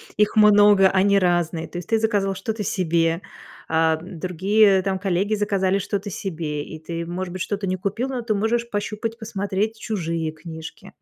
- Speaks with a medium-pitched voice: No, high, 195 Hz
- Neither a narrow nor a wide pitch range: Yes, average, 3.4 semitones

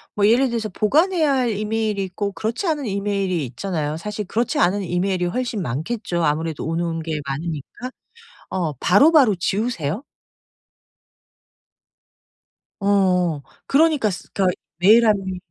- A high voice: Yes, high, 200 Hz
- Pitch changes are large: No, average, 4.8 semitones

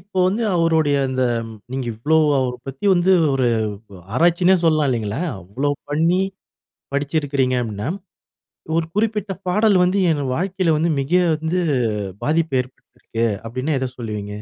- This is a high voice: No, medium, 150 Hz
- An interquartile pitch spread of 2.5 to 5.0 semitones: No, wide, 5.5 semitones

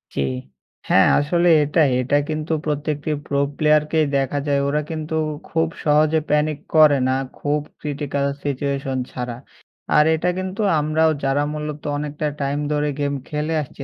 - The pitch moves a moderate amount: No, narrow, 1.5 semitones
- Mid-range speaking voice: Yes, medium, 150 Hz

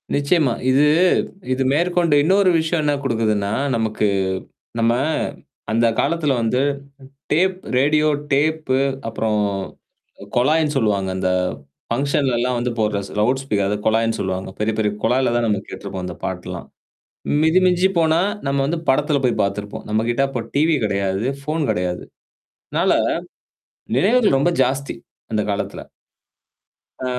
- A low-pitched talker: Yes, low, 130 Hz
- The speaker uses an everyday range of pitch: No, wide, 6.1 semitones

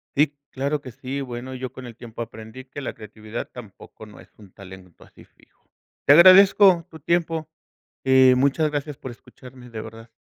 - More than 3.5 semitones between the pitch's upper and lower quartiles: Yes, average, 4.4 semitones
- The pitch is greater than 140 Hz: No, low, 130 Hz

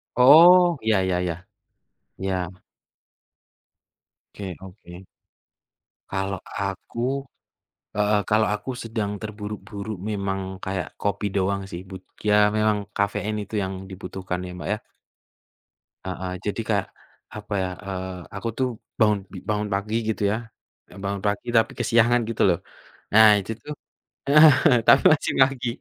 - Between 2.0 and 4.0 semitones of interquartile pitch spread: Yes, narrow, 2.4 semitones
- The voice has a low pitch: Yes, low, 105 Hz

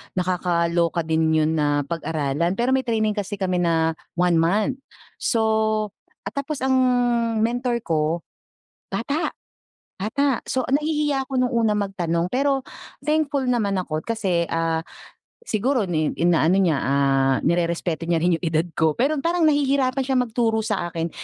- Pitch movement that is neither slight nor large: No, wide, 7.3 semitones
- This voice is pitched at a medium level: No, high, 195 Hz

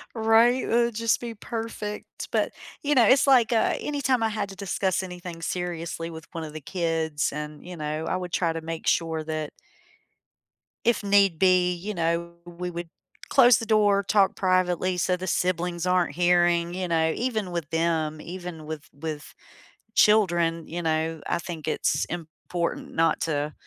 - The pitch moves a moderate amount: Yes, average, 3.8 semitones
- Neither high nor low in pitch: Yes, medium, 175 Hz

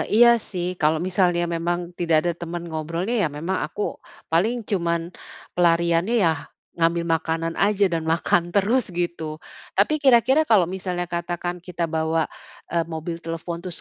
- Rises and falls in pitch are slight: Yes, narrow, 2.1 semitones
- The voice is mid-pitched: Yes, medium, 175 Hz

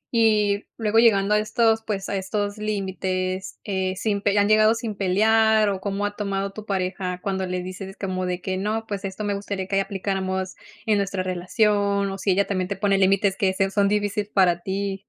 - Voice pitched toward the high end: Yes, high, 200 Hz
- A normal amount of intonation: No, narrow, 1.7 semitones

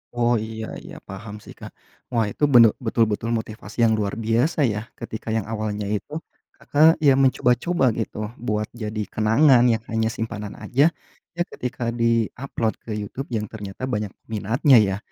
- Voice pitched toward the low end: Yes, low, 110 Hz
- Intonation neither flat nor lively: No, narrow, 2.3 semitones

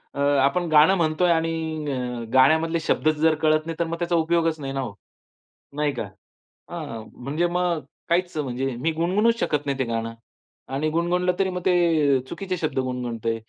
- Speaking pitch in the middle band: Yes, medium, 155 Hz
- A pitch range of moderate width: Yes, average, 4.0 semitones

